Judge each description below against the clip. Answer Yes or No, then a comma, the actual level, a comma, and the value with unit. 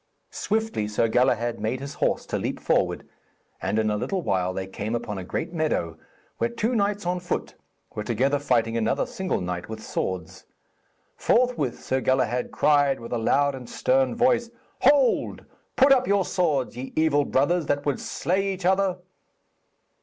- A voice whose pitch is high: No, medium, 140 Hz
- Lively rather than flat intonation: Yes, wide, 8.7 semitones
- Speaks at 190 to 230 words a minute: No, average, 170 wpm